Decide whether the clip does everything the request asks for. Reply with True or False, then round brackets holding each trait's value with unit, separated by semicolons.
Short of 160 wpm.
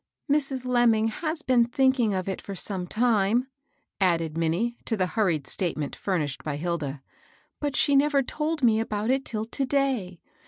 False (180 wpm)